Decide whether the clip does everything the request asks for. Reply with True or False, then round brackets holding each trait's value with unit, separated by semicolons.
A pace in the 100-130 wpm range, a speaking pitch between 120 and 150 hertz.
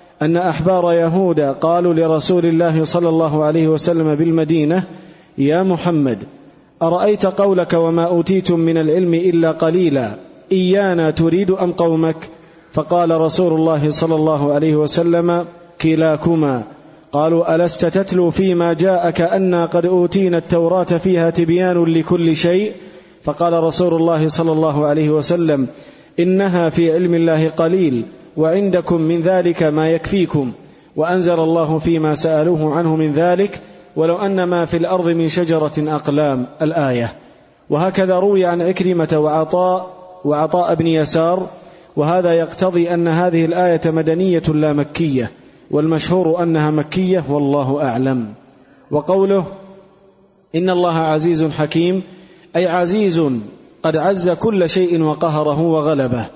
False (120 wpm; 165 Hz)